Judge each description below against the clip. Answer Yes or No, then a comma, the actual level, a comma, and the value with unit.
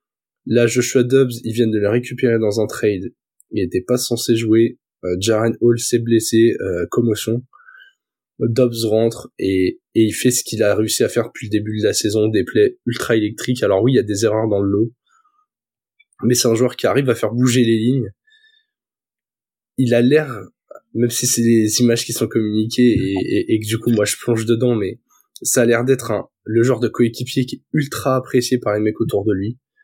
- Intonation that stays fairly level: Yes, narrow, 2.2 semitones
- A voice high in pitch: No, low, 120 Hz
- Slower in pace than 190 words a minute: No, average, 215 wpm